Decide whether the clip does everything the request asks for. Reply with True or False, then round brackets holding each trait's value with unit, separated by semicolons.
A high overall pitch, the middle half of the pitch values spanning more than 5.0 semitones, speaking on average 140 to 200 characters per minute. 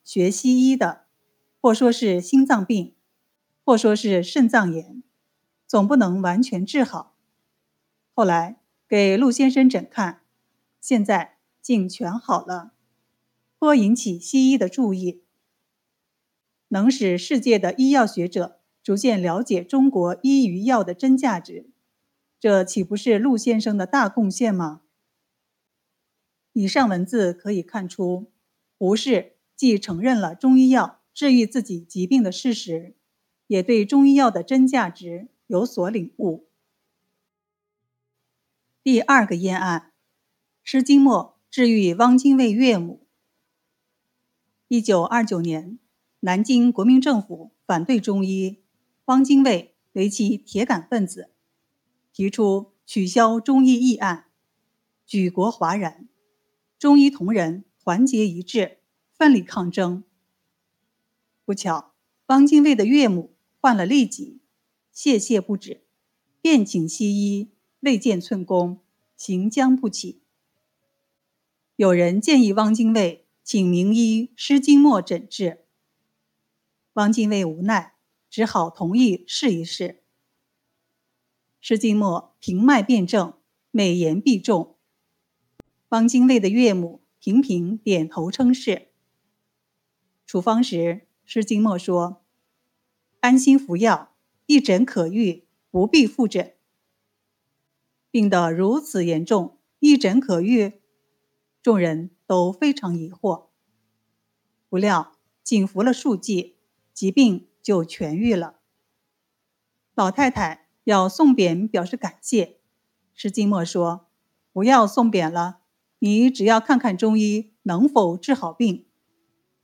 True (210 Hz; 5.4 semitones; 170 characters per minute)